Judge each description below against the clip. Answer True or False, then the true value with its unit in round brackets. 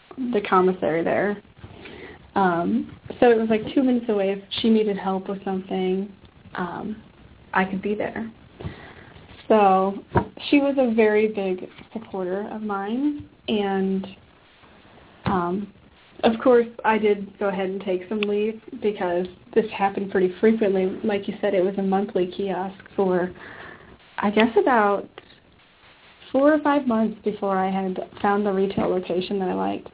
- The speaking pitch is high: True (200 Hz)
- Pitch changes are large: False (2.5 semitones)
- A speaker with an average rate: True (150 wpm)